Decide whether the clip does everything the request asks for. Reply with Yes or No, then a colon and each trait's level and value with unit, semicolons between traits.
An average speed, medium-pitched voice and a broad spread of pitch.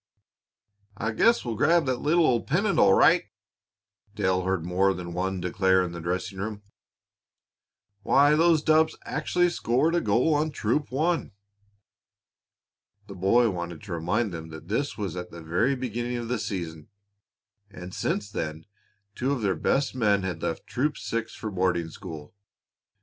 No: average, 160 wpm; low, 105 Hz; wide, 6.4 semitones